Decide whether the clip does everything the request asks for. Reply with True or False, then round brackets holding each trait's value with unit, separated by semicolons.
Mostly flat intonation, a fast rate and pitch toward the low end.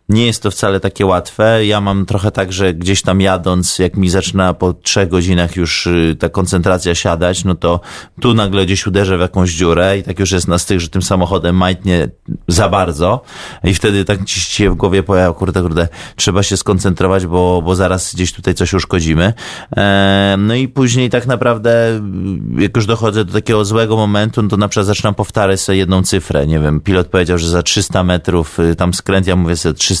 True (2.3 semitones; 200 wpm; 95 Hz)